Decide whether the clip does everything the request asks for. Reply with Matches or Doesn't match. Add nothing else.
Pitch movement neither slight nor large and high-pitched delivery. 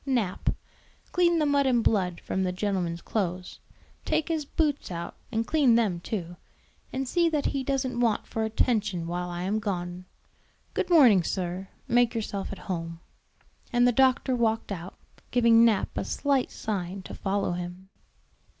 Doesn't match